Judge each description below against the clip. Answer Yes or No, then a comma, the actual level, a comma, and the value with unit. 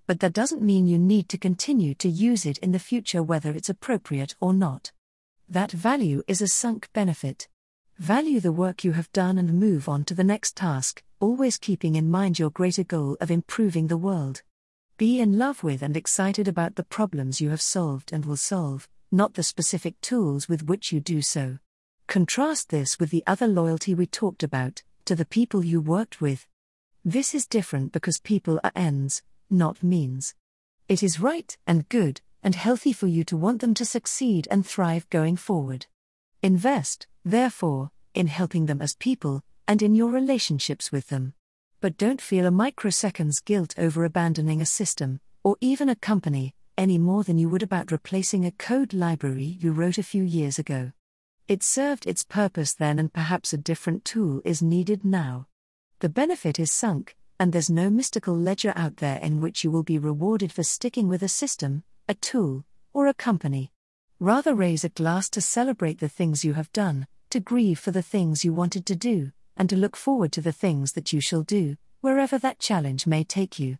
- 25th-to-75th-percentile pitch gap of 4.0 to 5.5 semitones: Yes, average, 4.9 semitones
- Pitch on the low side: No, medium, 175 Hz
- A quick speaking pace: No, average, 190 wpm